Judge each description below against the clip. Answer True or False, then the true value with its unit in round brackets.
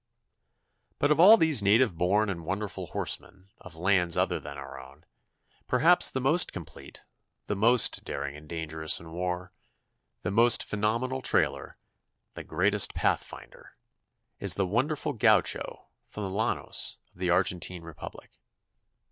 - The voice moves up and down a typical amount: False (5.9 semitones)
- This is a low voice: True (95 Hz)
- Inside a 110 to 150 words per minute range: True (140 wpm)